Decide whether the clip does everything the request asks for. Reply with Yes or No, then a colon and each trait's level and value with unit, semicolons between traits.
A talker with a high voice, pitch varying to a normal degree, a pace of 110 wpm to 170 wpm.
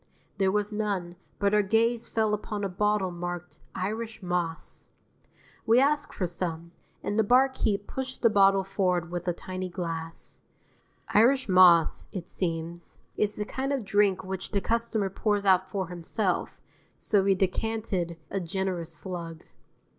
Yes: high, 195 Hz; average, 3.1 semitones; average, 150 wpm